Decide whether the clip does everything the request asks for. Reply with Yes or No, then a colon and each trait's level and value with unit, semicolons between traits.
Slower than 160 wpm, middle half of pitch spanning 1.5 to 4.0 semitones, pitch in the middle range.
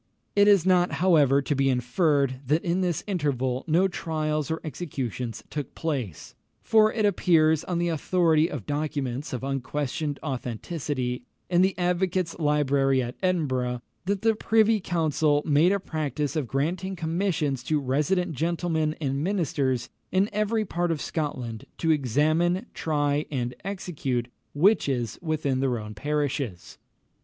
No: average, 140 wpm; average, 4.5 semitones; medium, 155 Hz